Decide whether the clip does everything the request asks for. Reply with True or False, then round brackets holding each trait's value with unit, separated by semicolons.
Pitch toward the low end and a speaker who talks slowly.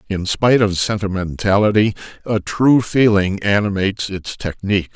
True (100 Hz; 120 wpm)